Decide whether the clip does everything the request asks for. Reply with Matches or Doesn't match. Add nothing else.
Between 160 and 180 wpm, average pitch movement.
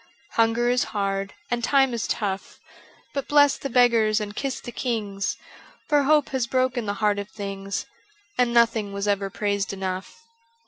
Matches